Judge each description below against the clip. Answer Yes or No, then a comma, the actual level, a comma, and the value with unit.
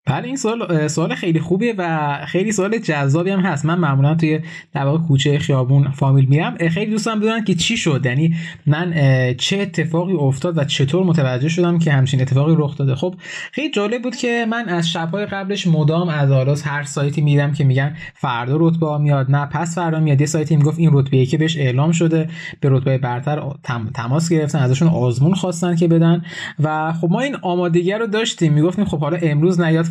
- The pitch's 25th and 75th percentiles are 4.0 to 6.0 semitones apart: No, average, 3.6 semitones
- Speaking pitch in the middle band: Yes, medium, 160 Hz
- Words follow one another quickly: Yes, fast, 195 wpm